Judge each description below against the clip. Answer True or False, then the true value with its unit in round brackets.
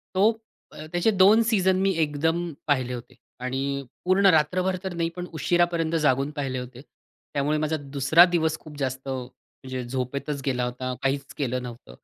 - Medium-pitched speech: True (145 Hz)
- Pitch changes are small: False (4.8 semitones)